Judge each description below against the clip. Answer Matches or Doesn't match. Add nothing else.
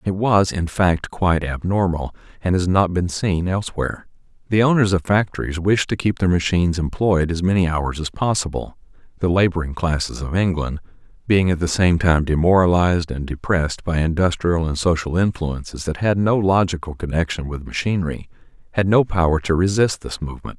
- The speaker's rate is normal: Matches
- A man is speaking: Matches